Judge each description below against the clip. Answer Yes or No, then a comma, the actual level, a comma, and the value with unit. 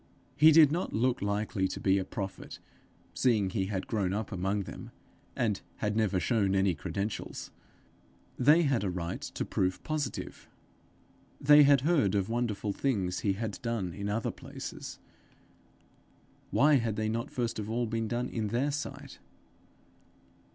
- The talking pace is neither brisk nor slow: Yes, average, 155 wpm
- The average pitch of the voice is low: Yes, low, 110 Hz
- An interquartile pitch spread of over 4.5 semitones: No, average, 4.2 semitones